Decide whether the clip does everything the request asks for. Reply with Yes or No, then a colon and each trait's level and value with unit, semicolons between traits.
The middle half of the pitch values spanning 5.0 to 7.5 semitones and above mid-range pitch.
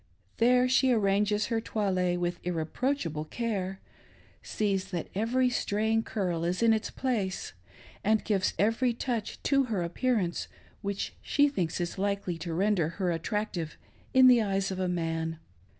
No: average, 4.3 semitones; high, 200 Hz